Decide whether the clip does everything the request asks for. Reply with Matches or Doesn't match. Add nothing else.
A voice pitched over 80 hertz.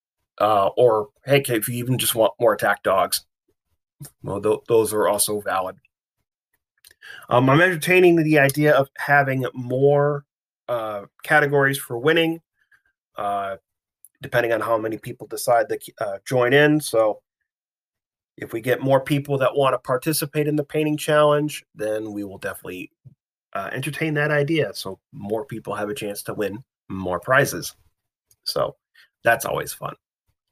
Matches